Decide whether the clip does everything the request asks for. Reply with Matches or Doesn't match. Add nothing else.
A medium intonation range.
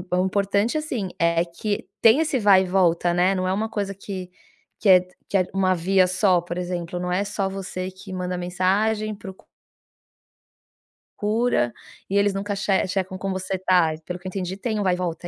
Doesn't match